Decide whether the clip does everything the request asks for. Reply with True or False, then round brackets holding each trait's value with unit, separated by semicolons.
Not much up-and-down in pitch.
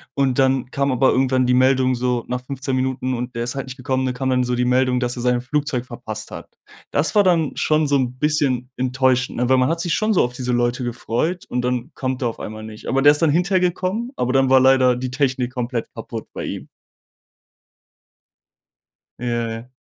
True (1.9 semitones)